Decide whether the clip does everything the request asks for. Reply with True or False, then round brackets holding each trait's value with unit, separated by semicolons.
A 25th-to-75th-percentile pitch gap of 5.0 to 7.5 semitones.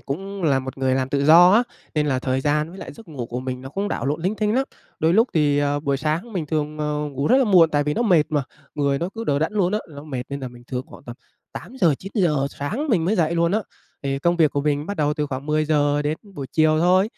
False (4.2 semitones)